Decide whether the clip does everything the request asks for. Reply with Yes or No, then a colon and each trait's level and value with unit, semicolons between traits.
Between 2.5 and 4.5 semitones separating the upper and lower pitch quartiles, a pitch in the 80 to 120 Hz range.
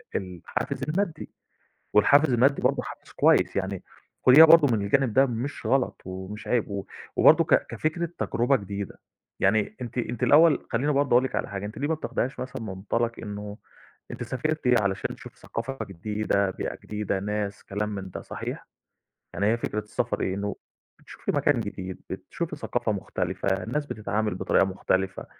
No: average, 4.9 semitones; low, 110 Hz